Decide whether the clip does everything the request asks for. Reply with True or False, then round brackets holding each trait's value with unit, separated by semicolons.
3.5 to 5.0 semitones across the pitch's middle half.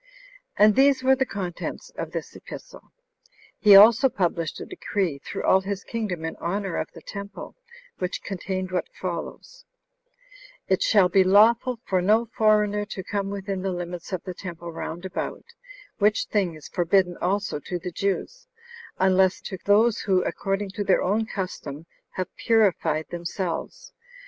False (2.7 semitones)